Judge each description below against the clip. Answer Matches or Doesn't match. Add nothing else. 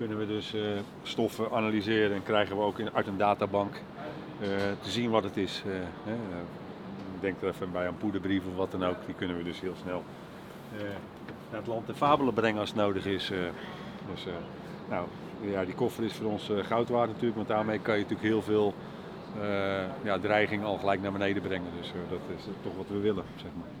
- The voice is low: Matches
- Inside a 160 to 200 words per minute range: Matches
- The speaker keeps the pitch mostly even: Matches